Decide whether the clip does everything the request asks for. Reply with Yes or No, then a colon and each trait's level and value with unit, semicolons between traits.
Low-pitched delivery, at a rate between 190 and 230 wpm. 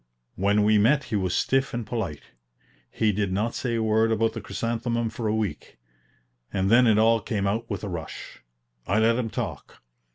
Yes: low, 110 Hz; average, 195 wpm